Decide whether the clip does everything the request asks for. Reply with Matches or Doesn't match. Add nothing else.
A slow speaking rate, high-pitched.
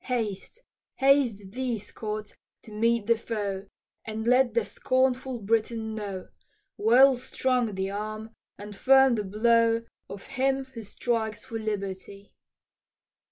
Matches